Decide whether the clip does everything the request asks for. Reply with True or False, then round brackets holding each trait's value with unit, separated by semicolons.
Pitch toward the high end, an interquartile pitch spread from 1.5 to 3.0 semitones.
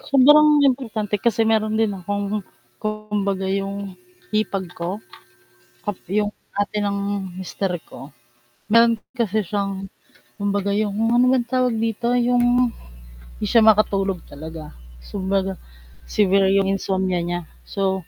True (205 Hz; 2.5 semitones)